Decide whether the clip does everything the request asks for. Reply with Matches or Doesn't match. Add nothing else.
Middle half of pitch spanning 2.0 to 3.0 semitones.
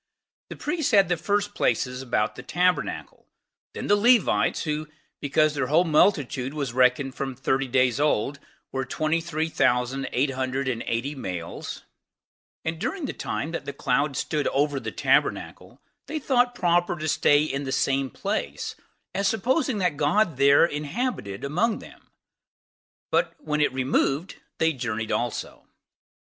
Doesn't match